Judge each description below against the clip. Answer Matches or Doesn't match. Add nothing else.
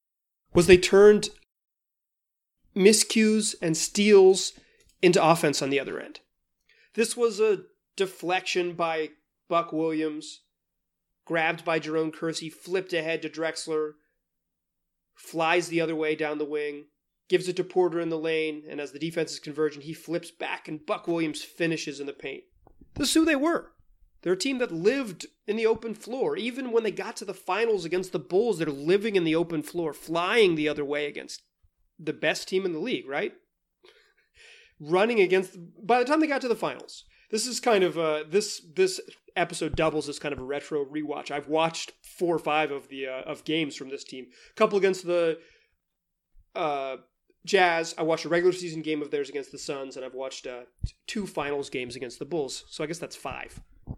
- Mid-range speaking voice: Matches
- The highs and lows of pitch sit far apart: Doesn't match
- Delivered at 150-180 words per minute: Doesn't match